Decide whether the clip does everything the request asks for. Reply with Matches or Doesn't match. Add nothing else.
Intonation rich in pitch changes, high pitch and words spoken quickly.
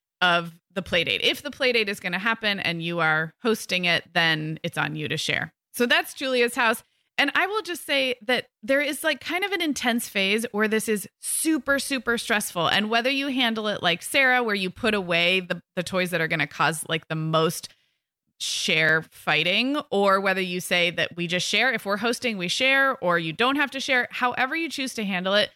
Matches